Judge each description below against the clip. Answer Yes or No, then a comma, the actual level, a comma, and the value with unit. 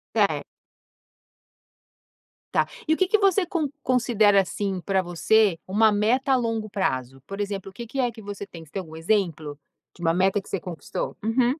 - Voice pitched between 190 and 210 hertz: Yes, high, 205 Hz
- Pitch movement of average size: Yes, average, 4.7 semitones